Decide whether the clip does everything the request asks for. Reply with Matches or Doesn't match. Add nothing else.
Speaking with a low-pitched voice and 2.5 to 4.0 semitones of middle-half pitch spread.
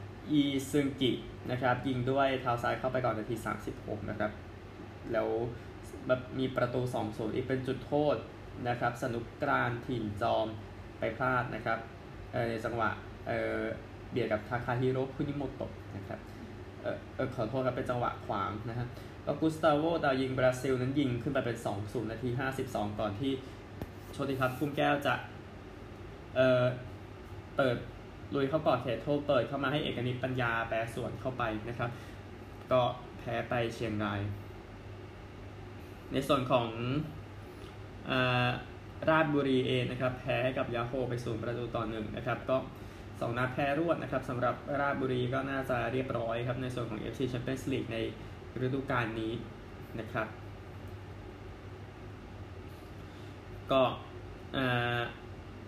Matches